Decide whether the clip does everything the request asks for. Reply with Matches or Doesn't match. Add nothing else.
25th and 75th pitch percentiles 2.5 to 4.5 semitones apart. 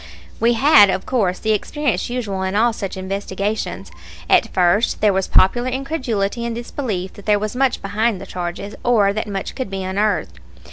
Matches